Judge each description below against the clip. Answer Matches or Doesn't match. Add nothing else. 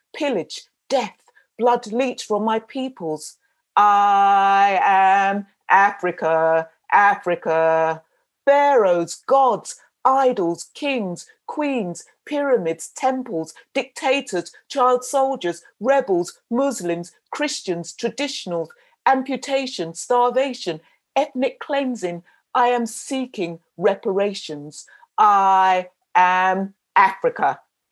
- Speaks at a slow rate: Matches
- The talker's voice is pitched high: Matches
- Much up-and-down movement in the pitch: Matches